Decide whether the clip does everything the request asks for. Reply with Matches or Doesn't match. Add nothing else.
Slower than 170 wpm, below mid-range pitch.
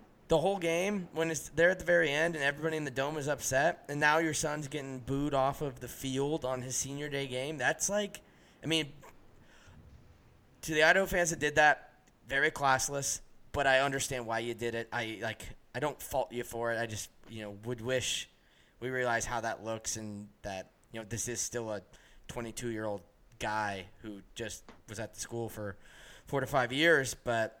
Doesn't match